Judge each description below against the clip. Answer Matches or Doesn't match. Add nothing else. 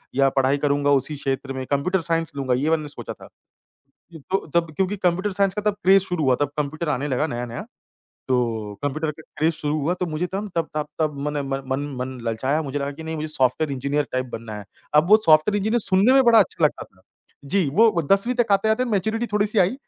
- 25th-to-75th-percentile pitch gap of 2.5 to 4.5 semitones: Doesn't match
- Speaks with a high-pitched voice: Doesn't match